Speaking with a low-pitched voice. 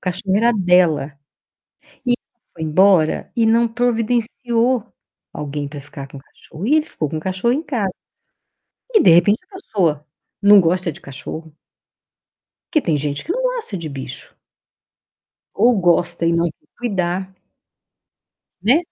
No: medium, 185 Hz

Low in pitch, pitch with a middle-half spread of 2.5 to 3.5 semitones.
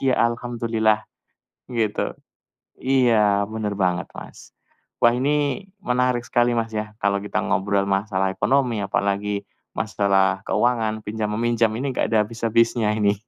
Yes: low, 110 Hz; average, 2.9 semitones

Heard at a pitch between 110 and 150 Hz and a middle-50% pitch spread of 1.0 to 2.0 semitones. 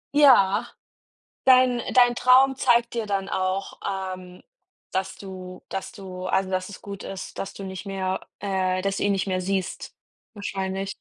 No: high, 195 Hz; narrow, 1.7 semitones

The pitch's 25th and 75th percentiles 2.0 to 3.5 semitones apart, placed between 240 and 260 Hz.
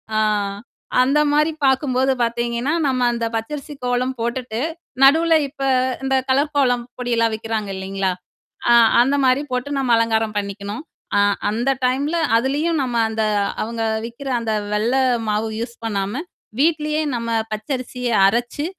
Yes: average, 3.2 semitones; high, 245 Hz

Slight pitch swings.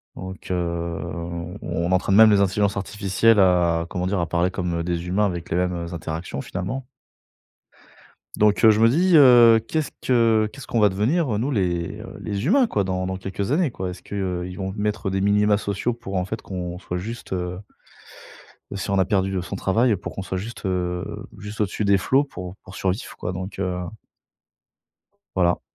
No: average, 3.2 semitones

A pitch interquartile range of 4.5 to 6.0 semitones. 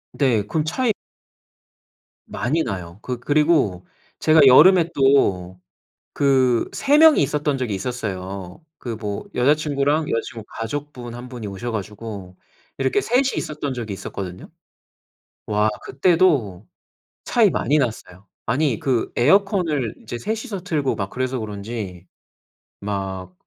No: wide, 6.6 semitones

